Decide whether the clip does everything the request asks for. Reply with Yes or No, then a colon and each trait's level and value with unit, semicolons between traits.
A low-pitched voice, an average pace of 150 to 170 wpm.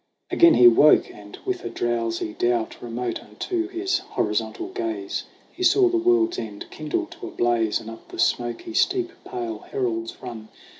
Yes: low, 125 Hz; average, 165 wpm